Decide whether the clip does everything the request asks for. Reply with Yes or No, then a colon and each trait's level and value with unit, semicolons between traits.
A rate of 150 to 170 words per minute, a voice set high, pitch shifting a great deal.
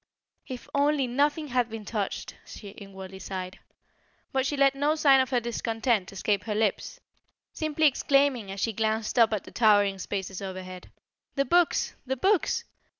Yes: average, 160 wpm; high, 230 Hz; wide, 5.7 semitones